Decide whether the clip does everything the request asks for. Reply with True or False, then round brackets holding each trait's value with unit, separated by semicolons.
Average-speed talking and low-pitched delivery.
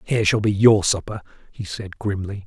True (195 wpm; 100 Hz)